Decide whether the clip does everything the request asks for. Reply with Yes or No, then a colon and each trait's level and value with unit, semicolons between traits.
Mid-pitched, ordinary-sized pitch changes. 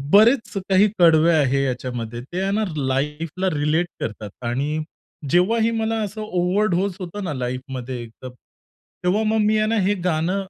No: medium, 175 Hz; wide, 7.4 semitones